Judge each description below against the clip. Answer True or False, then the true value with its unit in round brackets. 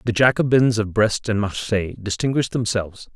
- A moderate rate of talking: True (150 wpm)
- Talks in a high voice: False (110 Hz)